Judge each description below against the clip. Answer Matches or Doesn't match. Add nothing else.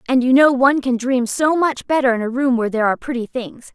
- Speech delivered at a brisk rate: Matches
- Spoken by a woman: Matches